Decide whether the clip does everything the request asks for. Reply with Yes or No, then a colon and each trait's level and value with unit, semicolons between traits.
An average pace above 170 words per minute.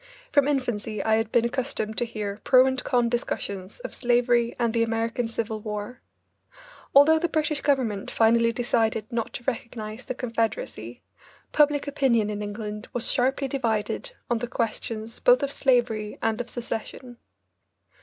No: average, 155 wpm